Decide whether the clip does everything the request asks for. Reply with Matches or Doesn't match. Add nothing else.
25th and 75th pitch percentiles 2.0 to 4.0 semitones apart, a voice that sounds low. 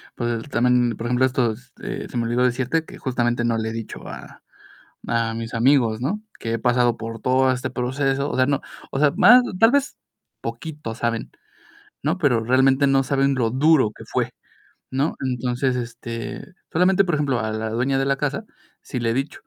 Matches